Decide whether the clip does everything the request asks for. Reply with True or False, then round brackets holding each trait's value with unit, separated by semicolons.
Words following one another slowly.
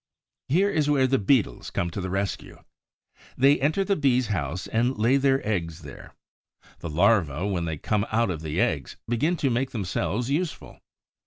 False (175 wpm)